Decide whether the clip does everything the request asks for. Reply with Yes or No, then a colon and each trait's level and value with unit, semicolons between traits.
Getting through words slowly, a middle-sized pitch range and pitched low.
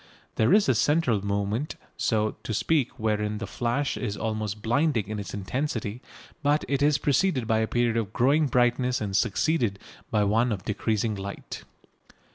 No: average, 165 wpm; average, 4.2 semitones; low, 115 Hz